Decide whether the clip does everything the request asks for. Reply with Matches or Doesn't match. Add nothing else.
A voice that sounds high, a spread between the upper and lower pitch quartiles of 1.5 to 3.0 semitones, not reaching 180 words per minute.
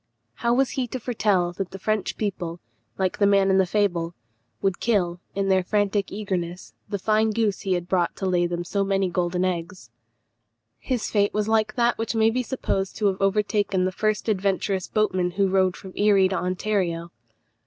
Doesn't match